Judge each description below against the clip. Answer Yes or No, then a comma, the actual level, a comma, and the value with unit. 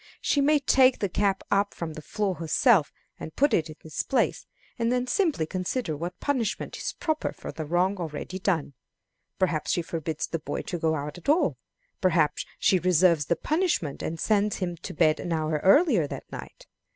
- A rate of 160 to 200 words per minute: Yes, average, 190 wpm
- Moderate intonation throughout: No, wide, 6.2 semitones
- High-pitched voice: No, medium, 180 Hz